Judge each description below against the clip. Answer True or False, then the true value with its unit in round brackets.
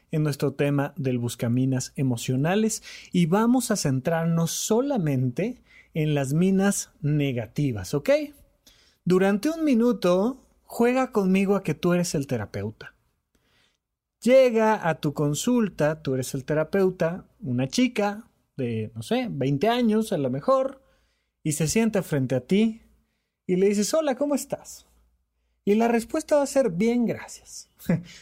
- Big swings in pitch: True (8.3 semitones)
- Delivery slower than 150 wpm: True (140 wpm)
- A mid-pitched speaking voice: True (175 Hz)